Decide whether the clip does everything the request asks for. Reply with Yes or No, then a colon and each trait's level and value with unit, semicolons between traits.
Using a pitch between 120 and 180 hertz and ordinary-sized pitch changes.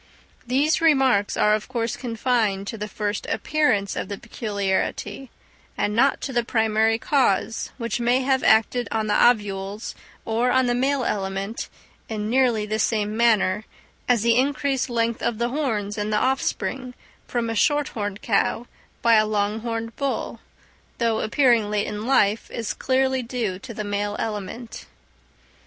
No: high, 225 Hz; average, 3.1 semitones